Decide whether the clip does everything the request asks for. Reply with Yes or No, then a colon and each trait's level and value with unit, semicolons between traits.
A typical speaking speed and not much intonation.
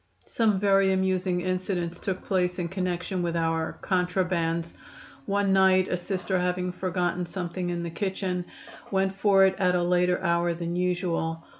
Yes: average, 155 wpm; narrow, 1.5 semitones